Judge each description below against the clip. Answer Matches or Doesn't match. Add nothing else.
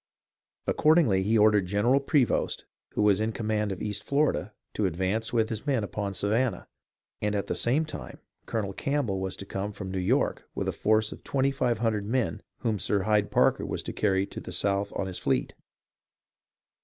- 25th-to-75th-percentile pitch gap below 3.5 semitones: Matches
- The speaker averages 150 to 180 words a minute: Doesn't match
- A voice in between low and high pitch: Doesn't match